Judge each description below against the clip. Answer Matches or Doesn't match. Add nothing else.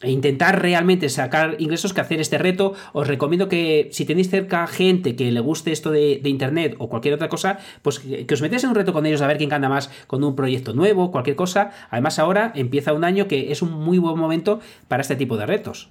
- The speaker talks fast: Matches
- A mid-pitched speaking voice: Matches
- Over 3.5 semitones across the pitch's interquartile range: Matches